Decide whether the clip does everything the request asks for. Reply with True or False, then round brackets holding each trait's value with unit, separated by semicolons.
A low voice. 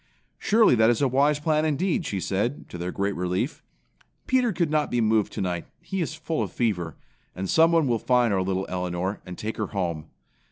True (110 Hz)